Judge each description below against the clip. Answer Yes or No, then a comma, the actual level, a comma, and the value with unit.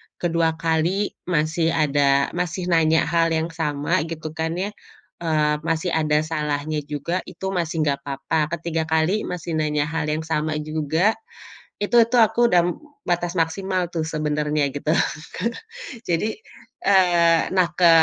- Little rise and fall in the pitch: Yes, narrow, 2.3 semitones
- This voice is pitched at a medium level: Yes, medium, 160 Hz